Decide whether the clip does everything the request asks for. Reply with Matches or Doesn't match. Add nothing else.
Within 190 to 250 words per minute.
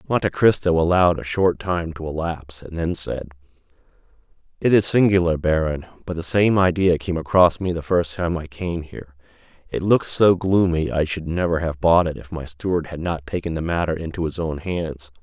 Matches